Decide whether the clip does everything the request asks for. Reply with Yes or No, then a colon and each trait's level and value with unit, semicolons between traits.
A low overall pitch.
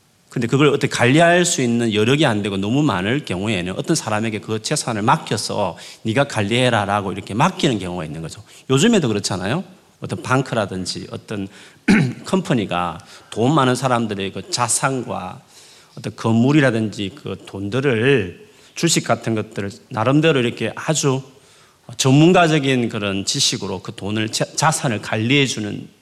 Yes: low, 120 Hz